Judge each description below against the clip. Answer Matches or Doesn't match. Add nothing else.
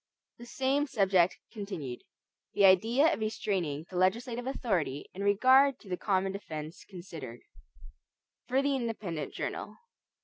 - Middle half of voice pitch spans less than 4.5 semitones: Doesn't match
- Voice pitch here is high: Matches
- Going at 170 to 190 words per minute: Doesn't match